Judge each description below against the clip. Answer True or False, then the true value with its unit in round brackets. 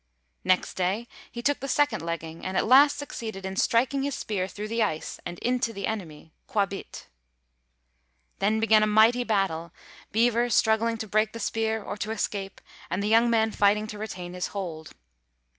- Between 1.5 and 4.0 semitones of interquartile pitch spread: True (3.2 semitones)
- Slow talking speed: False (175 wpm)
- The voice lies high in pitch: True (215 Hz)